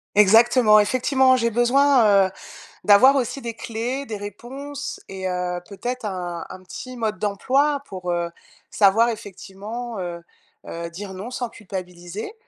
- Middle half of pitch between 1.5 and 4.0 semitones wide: No, average, 4.7 semitones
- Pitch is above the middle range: Yes, high, 215 Hz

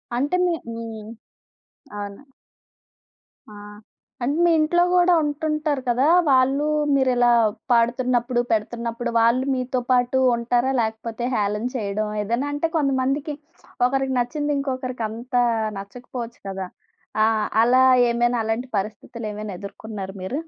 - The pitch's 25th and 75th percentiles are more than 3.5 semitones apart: No, average, 3.2 semitones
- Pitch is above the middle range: Yes, high, 245 Hz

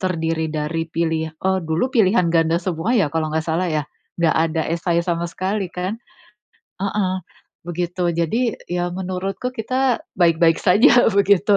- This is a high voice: No, medium, 175 Hz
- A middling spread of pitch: Yes, average, 3.1 semitones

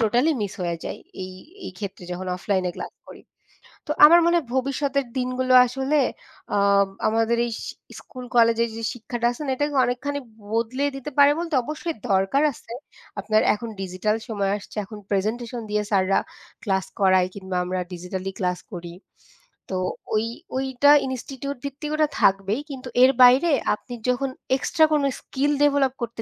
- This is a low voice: No, high, 235 Hz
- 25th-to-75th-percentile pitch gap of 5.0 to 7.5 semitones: Yes, wide, 5.6 semitones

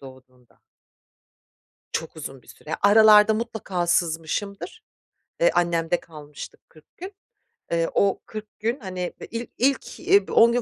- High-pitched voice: Yes, high, 195 Hz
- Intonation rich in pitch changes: Yes, wide, 6.0 semitones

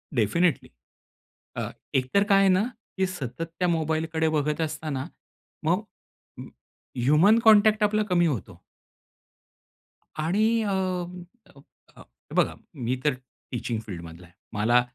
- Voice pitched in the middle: Yes, medium, 160 Hz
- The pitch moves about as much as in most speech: No, wide, 6.7 semitones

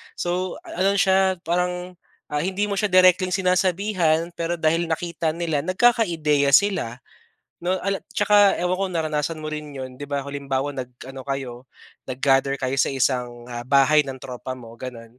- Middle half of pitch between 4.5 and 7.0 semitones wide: Yes, average, 5.3 semitones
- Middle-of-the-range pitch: Yes, medium, 160 Hz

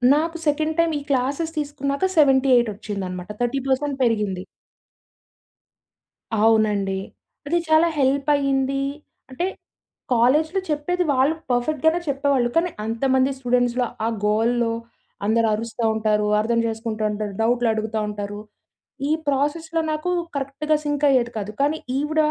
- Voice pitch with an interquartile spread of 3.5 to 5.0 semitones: Yes, average, 4.7 semitones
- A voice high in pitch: Yes, very high, 260 Hz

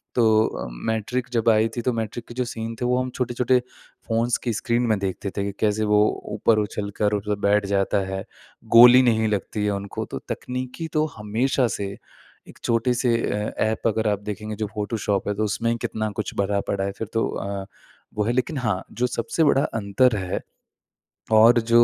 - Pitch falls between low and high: No, low, 110 Hz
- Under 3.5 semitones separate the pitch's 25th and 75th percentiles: Yes, average, 2.7 semitones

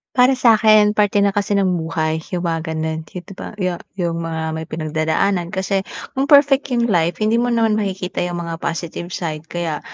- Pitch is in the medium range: Yes, medium, 180 Hz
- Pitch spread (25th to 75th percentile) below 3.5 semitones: No, average, 4.5 semitones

